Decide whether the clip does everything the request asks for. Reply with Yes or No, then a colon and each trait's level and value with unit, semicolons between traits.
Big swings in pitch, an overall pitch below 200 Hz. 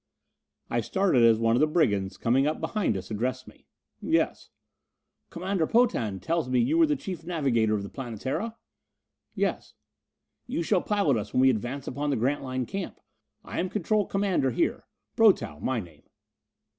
Yes: wide, 8.1 semitones; low, 135 Hz